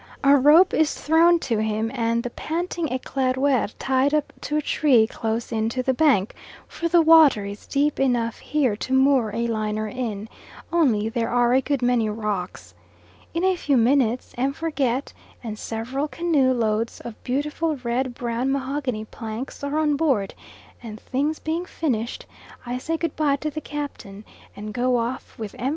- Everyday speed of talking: Yes, average, 170 wpm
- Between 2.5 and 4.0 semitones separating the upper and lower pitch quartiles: No, average, 4.4 semitones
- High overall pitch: Yes, very high, 255 Hz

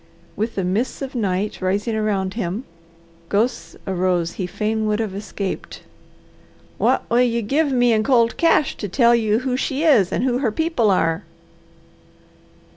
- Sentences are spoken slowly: No, average, 160 wpm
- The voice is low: No, high, 220 Hz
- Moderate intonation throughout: Yes, average, 4.1 semitones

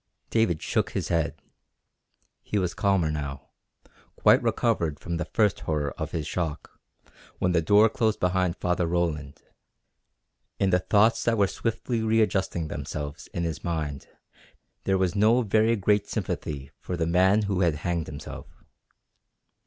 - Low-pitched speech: Yes, very low, 90 Hz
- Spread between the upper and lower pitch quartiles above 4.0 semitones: Yes, average, 4.5 semitones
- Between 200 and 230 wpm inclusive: No, average, 145 wpm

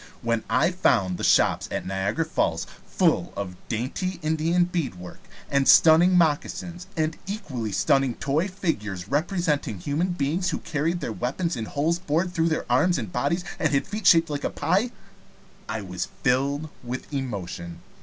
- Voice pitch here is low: No, medium, 145 Hz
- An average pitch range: No, wide, 6.8 semitones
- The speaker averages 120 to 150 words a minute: No, average, 160 wpm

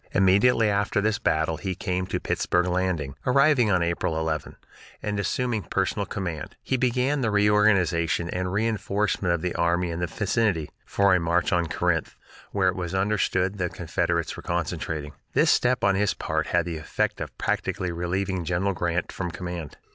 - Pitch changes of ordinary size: Yes, average, 3.2 semitones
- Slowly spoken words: No, average, 170 wpm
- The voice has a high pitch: No, very low, 90 Hz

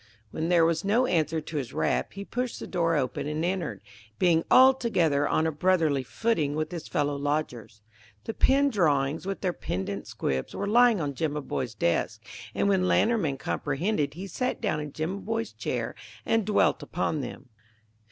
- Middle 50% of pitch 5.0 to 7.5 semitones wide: Yes, wide, 5.5 semitones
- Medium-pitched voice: Yes, medium, 165 Hz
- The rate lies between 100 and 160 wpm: No, average, 170 wpm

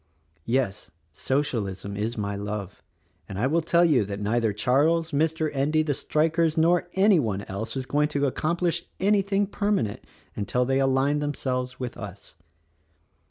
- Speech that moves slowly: No, average, 155 wpm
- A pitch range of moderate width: No, wide, 7.1 semitones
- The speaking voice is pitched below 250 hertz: Yes, low, 135 Hz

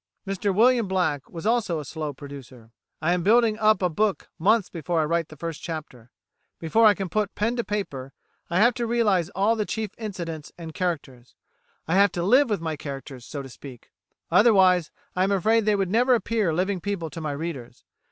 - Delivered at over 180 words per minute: Yes, average, 200 wpm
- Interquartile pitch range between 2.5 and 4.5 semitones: No, average, 5.3 semitones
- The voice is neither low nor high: Yes, medium, 180 Hz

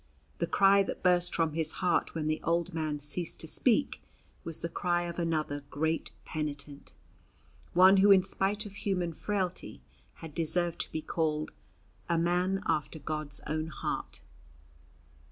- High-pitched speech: No, medium, 165 Hz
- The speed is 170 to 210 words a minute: No, average, 155 wpm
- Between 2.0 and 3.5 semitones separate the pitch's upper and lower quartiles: Yes, average, 2.8 semitones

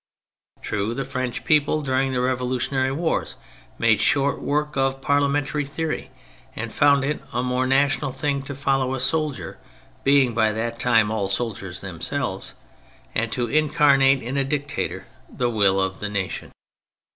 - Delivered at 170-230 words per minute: No, average, 155 wpm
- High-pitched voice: No, low, 130 Hz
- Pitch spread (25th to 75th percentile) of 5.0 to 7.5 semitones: No, average, 3.4 semitones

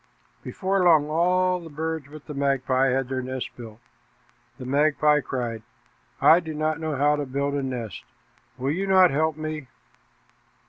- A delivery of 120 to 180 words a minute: Yes, average, 165 wpm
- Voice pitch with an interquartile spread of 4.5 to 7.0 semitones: No, average, 3.3 semitones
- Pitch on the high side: No, medium, 150 Hz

